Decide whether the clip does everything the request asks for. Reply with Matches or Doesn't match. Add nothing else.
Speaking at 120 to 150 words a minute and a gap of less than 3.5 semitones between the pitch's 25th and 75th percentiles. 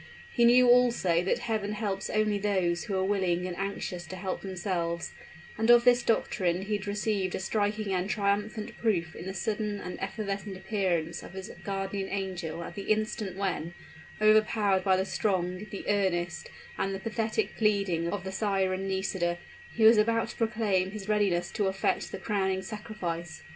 Doesn't match